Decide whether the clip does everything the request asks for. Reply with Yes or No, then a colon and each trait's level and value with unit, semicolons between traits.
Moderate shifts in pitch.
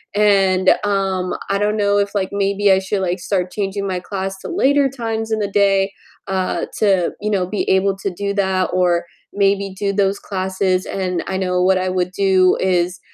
No: narrow, 1.4 semitones